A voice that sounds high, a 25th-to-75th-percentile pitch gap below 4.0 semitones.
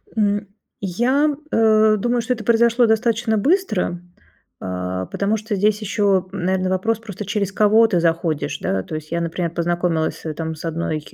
No: high, 200 Hz; average, 4.7 semitones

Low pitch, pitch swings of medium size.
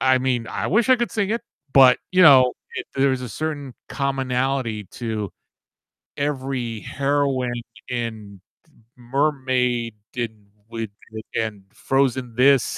Yes: low, 130 Hz; average, 3.0 semitones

